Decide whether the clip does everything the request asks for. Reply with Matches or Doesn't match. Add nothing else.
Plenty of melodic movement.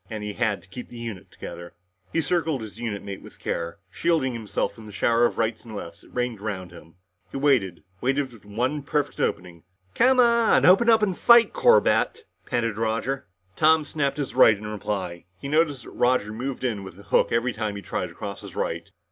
Matches